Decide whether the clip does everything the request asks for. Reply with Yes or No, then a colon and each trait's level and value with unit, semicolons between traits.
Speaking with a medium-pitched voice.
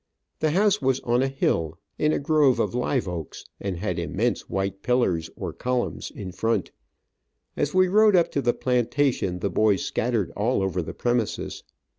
No: low, 120 Hz